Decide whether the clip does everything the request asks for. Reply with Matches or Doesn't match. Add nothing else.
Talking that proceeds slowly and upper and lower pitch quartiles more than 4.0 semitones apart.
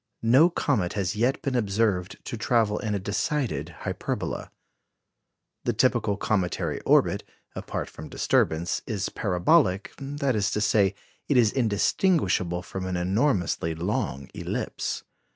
Matches